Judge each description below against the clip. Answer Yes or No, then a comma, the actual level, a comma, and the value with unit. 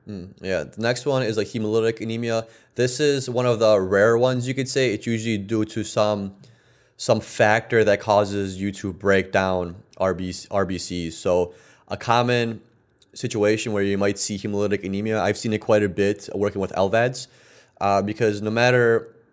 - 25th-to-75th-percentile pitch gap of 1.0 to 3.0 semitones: Yes, average, 2.7 semitones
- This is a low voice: Yes, low, 105 Hz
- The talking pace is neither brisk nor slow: Yes, average, 175 wpm